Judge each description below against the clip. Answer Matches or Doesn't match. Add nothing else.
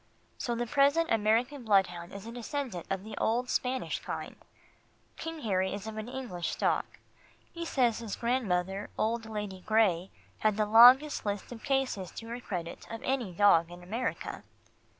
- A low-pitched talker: Doesn't match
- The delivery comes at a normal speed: Matches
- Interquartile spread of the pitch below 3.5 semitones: Doesn't match